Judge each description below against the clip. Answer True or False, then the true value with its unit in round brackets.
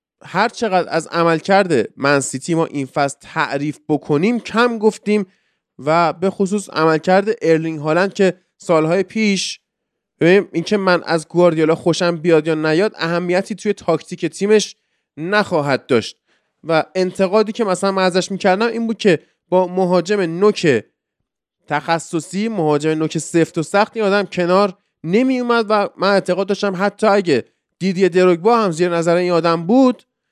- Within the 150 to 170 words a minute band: True (155 wpm)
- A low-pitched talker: False (185 Hz)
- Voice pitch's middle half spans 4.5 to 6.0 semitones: False (3.6 semitones)